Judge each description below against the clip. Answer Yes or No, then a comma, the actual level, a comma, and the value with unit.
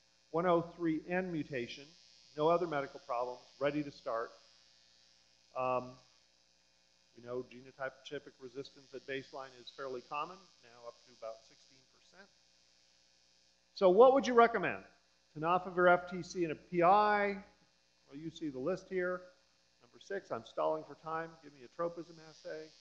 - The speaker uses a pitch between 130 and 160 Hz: Yes, medium, 140 Hz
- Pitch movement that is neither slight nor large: No, wide, 7.1 semitones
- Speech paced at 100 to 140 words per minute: Yes, slow, 135 wpm